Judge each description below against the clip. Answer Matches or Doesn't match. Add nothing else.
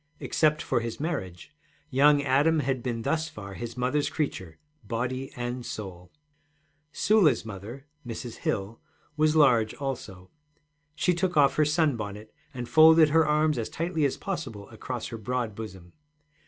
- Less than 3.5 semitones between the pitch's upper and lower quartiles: Doesn't match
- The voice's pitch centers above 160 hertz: Doesn't match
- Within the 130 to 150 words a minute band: Matches